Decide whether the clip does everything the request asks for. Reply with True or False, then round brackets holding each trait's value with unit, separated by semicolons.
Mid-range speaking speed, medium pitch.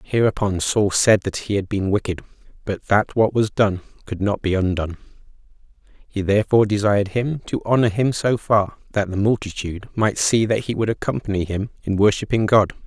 False (180 wpm; 105 Hz)